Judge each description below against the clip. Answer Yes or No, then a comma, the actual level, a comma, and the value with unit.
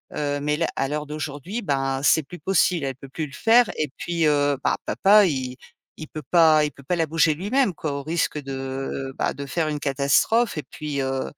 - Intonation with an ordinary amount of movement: Yes, average, 3.3 semitones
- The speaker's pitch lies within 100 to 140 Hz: No, medium, 150 Hz